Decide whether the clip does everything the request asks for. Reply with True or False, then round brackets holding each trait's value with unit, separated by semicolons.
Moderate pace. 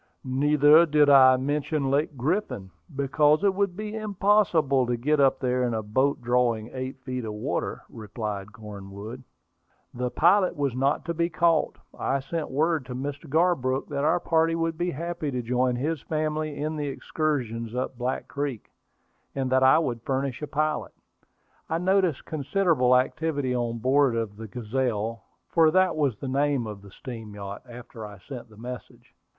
True (170 wpm)